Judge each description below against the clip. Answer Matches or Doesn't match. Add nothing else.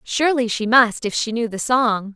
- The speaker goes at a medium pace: Doesn't match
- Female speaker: Matches